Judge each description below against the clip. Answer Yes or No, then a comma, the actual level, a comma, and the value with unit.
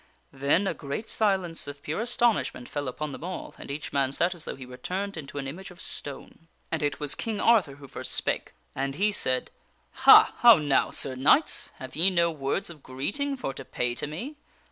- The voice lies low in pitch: No, medium, 155 Hz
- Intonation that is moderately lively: No, wide, 6.0 semitones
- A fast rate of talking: Yes, fast, 220 wpm